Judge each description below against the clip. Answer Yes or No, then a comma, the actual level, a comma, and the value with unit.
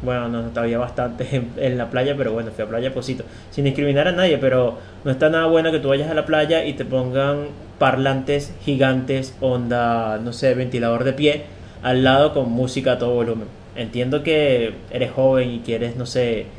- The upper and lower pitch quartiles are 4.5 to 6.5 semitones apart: No, average, 2.8 semitones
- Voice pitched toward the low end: Yes, low, 125 Hz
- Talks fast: Yes, fast, 205 wpm